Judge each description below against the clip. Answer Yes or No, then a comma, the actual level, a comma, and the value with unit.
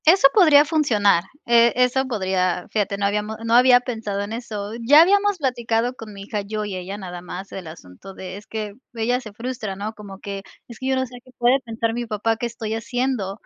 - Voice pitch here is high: Yes, high, 225 Hz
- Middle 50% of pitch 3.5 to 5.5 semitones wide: Yes, average, 3.8 semitones